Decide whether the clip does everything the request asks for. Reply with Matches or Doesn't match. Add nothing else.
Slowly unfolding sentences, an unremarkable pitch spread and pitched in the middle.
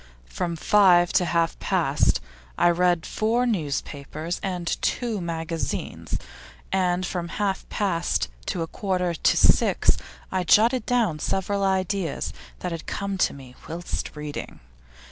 Matches